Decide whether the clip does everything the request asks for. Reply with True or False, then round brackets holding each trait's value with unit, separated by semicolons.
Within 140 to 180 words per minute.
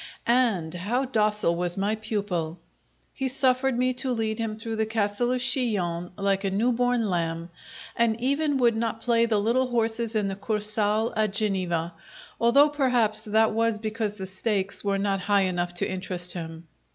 True (175 wpm)